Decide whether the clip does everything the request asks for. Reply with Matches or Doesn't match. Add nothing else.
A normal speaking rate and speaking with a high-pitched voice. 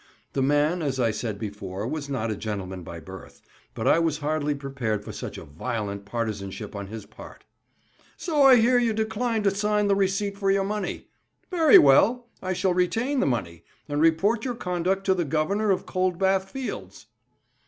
Doesn't match